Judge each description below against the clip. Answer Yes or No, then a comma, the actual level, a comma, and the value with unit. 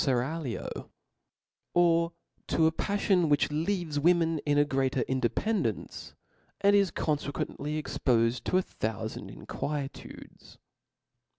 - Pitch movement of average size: Yes, average, 4.4 semitones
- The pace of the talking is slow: Yes, slow, 110 wpm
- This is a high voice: No, medium, 150 Hz